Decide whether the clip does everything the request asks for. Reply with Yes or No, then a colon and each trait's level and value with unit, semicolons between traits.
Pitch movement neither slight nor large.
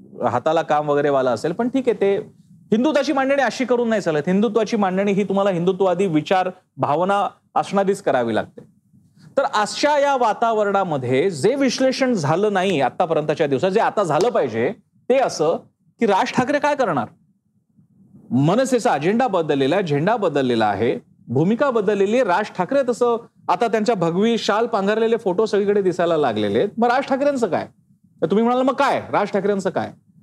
Yes: average, 4.8 semitones